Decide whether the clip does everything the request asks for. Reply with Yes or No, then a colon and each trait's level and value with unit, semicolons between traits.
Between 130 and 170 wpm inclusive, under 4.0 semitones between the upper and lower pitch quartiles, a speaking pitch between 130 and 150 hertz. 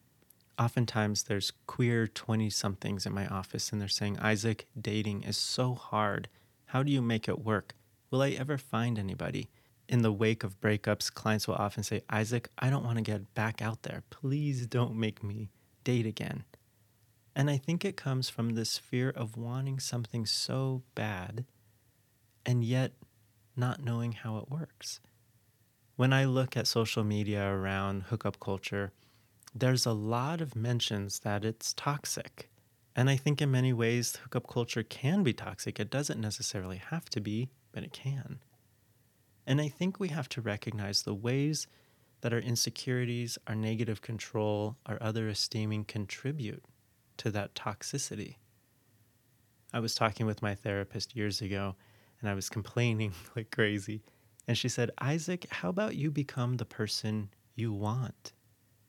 No: average, 160 wpm; average, 2.8 semitones; low, 115 Hz